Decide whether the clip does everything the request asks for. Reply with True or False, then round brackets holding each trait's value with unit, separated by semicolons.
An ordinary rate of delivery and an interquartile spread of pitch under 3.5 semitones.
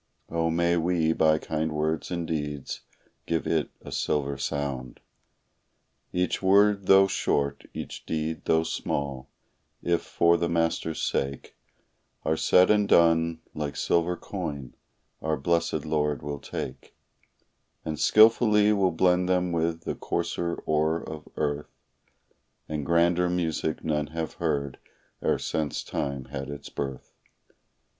False (130 wpm; 2.7 semitones)